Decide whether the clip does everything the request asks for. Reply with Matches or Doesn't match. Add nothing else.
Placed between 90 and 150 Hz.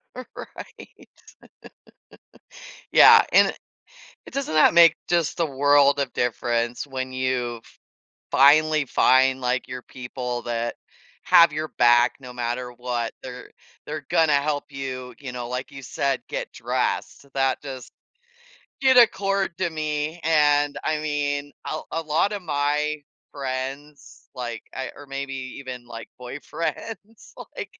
Matches